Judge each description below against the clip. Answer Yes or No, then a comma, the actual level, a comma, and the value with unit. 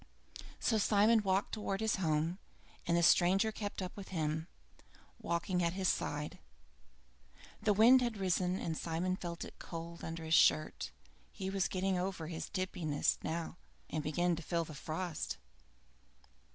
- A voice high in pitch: No, medium, 180 Hz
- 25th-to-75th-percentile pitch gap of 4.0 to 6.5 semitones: No, average, 3.0 semitones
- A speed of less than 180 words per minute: Yes, average, 155 wpm